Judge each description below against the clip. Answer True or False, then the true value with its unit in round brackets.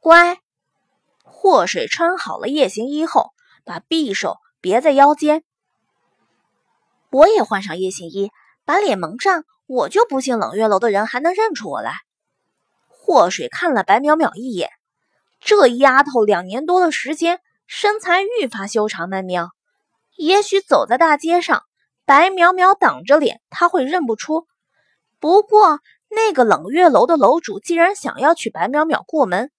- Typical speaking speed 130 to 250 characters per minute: True (215 characters per minute)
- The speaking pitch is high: True (310 Hz)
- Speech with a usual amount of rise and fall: False (6.7 semitones)